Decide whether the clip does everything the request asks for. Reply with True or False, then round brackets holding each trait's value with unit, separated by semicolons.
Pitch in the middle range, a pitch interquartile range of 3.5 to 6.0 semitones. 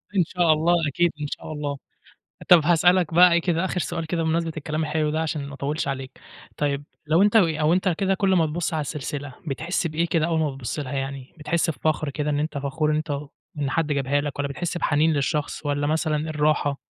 False (155 Hz; 2.6 semitones)